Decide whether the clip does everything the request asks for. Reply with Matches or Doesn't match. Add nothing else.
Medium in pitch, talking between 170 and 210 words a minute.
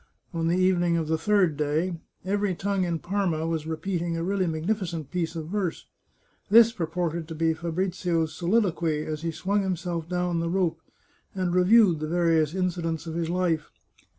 Matches